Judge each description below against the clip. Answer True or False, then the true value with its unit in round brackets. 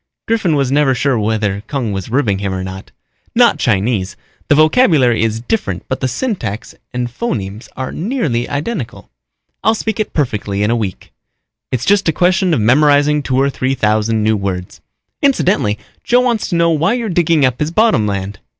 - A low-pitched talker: True (130 Hz)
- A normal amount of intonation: False (7.9 semitones)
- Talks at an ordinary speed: True (180 wpm)